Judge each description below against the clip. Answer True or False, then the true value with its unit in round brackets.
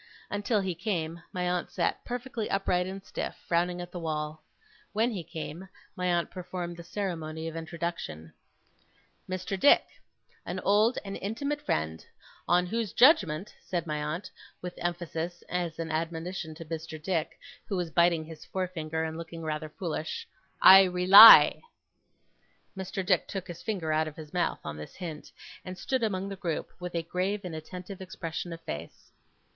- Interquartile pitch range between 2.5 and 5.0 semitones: True (2.9 semitones)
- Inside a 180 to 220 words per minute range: False (165 wpm)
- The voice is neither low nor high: True (175 Hz)